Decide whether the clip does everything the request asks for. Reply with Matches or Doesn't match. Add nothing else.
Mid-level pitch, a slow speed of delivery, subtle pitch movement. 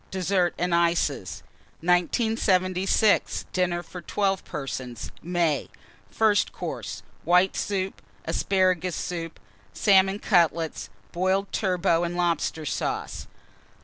Matches